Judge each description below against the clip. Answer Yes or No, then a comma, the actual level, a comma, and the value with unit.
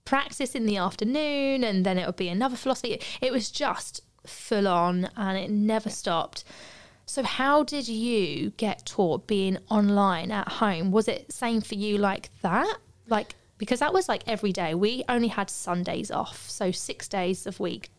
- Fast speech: No, average, 180 wpm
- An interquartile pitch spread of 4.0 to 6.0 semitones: Yes, average, 4.4 semitones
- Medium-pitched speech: No, high, 210 Hz